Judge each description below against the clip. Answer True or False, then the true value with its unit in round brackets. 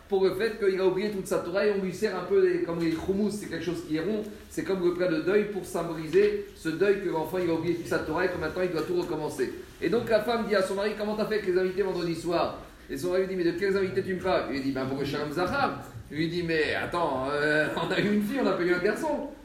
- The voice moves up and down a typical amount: True (3.4 semitones)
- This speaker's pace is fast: True (310 wpm)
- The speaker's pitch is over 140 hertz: True (185 Hz)